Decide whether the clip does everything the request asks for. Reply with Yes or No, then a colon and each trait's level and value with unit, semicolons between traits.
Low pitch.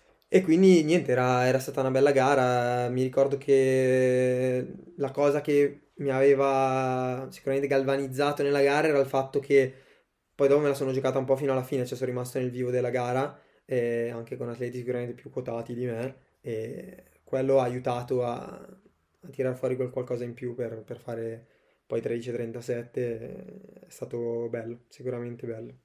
Yes: low, 130 Hz